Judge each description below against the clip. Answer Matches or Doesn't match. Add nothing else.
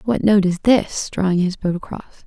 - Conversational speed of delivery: Doesn't match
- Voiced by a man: Doesn't match